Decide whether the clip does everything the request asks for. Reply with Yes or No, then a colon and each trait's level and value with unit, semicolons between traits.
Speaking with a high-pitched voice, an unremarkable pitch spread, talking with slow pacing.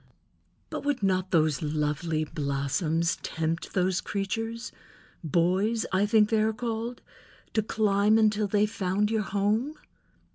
Yes: high, 200 Hz; average, 4.7 semitones; slow, 115 wpm